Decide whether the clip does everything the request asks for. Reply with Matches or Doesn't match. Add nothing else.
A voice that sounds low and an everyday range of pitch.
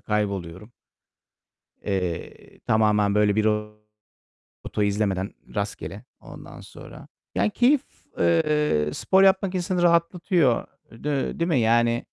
Doesn't match